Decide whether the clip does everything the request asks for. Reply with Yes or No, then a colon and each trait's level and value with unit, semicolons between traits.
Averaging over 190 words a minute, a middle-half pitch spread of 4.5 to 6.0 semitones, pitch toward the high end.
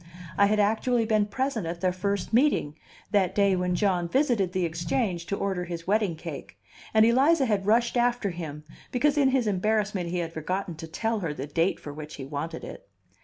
Yes: average, 200 wpm; average, 4.8 semitones; high, 195 Hz